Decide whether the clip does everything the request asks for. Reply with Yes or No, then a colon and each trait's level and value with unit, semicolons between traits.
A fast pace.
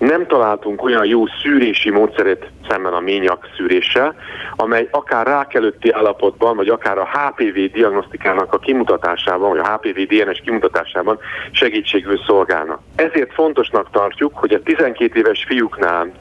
No: average, 135 wpm